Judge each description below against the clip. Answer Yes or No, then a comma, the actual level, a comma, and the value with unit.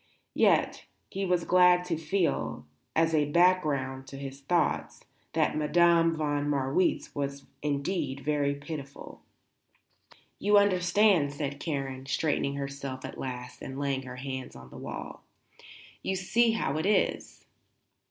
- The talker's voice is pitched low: No, medium, 145 Hz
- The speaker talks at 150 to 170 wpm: No, slow, 135 wpm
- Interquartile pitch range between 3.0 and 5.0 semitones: Yes, average, 4.2 semitones